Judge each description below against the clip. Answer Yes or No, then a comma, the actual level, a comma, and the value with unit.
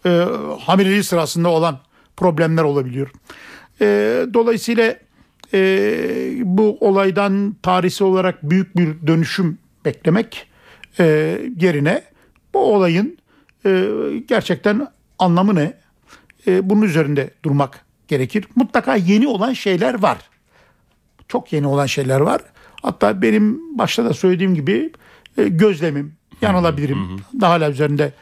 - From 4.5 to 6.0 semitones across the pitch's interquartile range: Yes, wide, 5.4 semitones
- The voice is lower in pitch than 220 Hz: Yes, medium, 185 Hz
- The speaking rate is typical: Yes, average, 110 wpm